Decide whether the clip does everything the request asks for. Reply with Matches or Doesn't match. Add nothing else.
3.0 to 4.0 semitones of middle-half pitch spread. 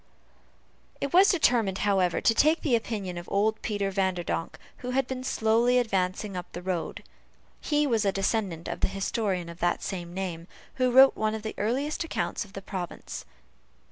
Doesn't match